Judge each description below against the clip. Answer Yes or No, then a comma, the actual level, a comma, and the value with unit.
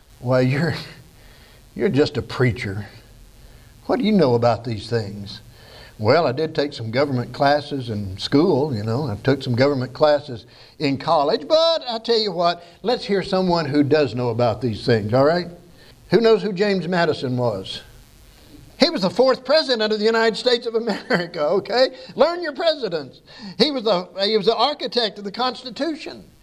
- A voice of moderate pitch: Yes, medium, 150 Hz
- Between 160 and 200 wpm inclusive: Yes, average, 175 wpm